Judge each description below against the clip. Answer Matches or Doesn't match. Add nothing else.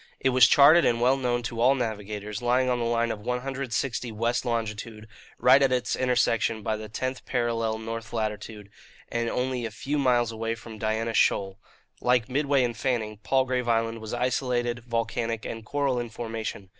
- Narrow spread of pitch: Matches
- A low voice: Matches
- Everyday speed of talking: Matches